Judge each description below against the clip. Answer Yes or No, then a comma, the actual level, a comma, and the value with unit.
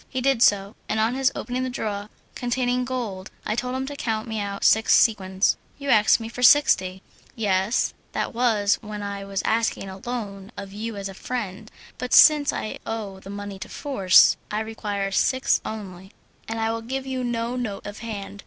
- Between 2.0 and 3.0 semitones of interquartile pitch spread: No, average, 3.6 semitones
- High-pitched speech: Yes, high, 220 Hz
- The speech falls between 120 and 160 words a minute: No, average, 195 wpm